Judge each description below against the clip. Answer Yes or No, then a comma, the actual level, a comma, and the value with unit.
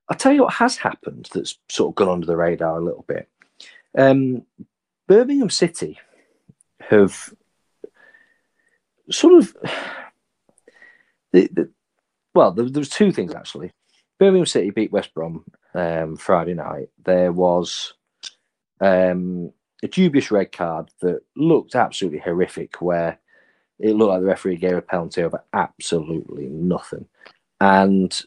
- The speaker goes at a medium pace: No, slow, 130 wpm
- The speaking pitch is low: Yes, low, 100 Hz